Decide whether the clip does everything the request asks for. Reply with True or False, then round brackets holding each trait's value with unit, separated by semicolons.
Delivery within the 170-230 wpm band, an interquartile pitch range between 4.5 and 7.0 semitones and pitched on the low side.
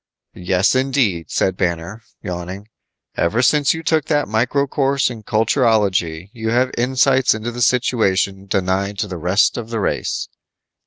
False (150 wpm; 5.1 semitones; 110 Hz)